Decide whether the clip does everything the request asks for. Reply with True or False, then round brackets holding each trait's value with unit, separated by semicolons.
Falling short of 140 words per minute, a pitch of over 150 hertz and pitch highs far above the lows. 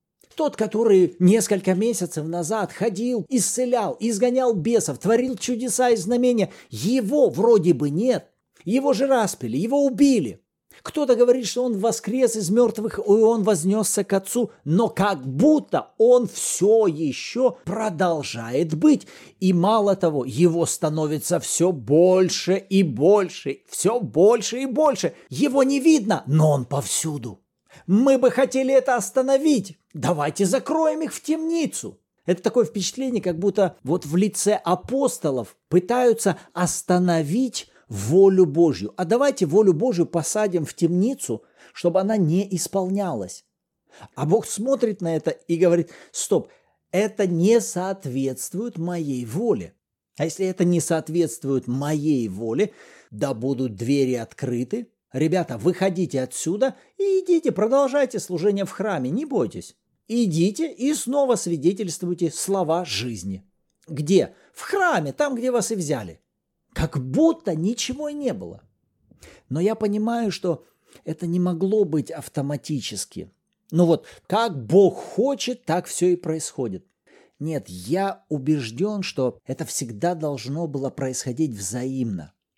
True (130 wpm; 190 Hz; 6.7 semitones)